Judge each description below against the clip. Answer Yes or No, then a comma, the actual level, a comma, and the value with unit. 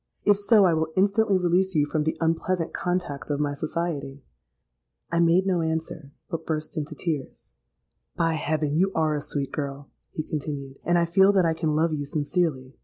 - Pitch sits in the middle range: Yes, medium, 160 Hz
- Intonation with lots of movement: No, average, 3.2 semitones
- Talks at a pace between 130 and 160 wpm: No, average, 180 wpm